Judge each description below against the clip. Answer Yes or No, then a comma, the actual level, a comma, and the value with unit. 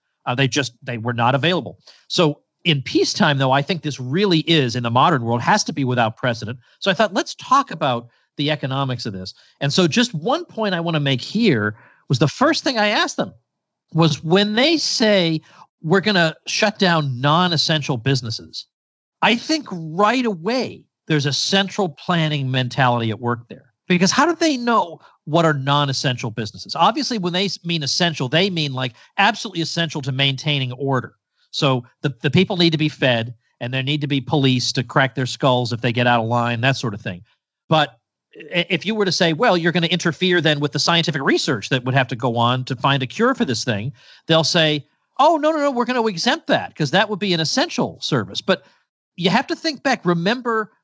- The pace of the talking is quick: Yes, fast, 210 wpm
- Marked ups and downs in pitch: Yes, wide, 7.2 semitones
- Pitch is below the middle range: No, medium, 155 Hz